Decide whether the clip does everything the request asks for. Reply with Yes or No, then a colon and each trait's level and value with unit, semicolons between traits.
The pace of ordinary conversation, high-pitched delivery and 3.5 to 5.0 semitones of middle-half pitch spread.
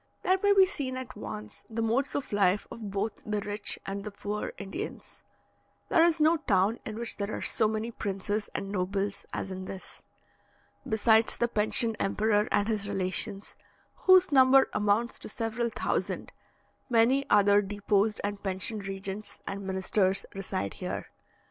No: average, 160 wpm; high, 210 Hz; average, 2.9 semitones